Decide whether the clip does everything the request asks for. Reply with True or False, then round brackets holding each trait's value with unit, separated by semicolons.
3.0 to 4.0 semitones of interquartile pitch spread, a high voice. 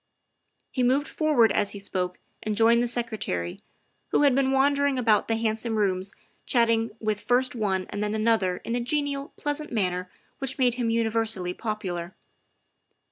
True (3.6 semitones; 225 Hz)